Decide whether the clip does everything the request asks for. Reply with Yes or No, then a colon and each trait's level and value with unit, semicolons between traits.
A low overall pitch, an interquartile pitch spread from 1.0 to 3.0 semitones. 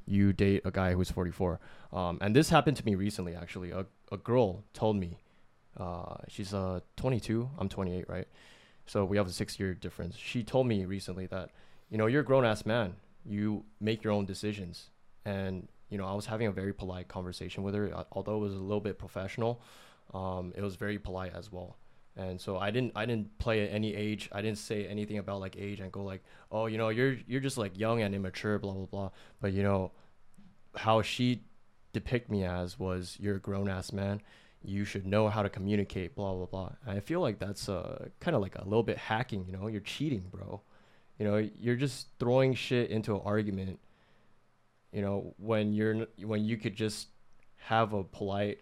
Yes: low, 100 Hz; narrow, 2.5 semitones